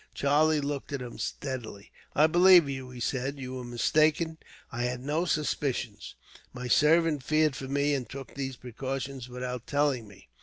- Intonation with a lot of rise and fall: No, average, 3.0 semitones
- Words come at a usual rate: Yes, average, 165 wpm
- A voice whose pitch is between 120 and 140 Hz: Yes, low, 135 Hz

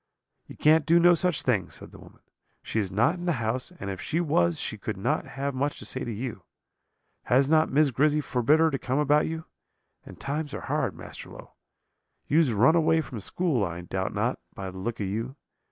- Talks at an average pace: No, fast, 220 wpm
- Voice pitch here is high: No, low, 135 Hz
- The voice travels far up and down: Yes, wide, 6.0 semitones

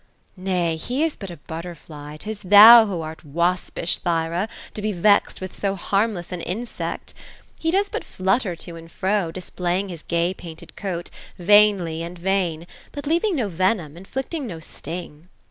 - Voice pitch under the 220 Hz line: Yes, medium, 185 Hz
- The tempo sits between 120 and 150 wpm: No, average, 165 wpm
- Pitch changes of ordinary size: Yes, average, 3.7 semitones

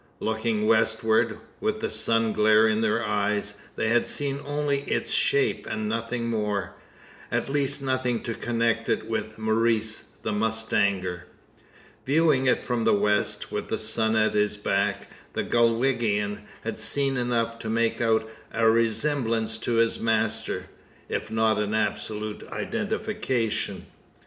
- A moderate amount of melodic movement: No, narrow, 1.5 semitones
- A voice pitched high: No, low, 110 Hz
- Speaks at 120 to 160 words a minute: Yes, average, 140 wpm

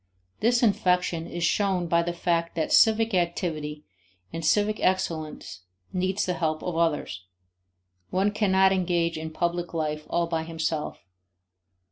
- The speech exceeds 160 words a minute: No, slow, 135 wpm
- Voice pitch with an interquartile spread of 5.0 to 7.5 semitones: No, average, 2.7 semitones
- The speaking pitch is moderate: Yes, medium, 170 Hz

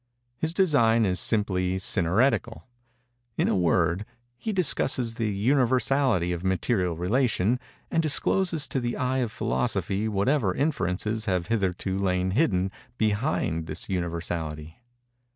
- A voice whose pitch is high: No, low, 105 Hz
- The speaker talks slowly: Yes, slow, 120 wpm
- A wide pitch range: Yes, wide, 5.7 semitones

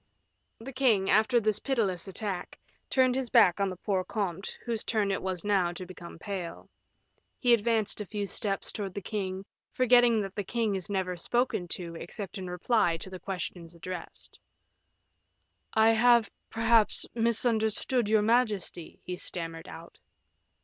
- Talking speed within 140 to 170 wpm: Yes, average, 150 wpm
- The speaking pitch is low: No, high, 205 Hz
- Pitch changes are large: No, average, 3.8 semitones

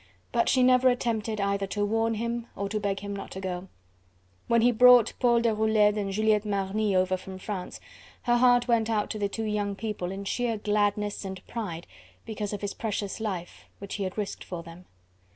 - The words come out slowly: No, average, 200 wpm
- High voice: Yes, high, 210 Hz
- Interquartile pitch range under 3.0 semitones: Yes, narrow, 2.4 semitones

